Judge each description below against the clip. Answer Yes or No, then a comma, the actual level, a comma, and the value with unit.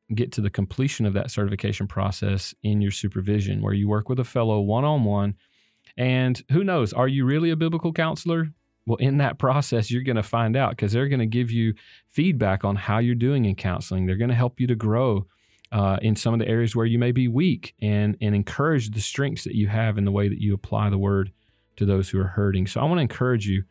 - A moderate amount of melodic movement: Yes, average, 4.0 semitones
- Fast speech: Yes, fast, 240 wpm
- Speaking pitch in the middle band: No, low, 110 Hz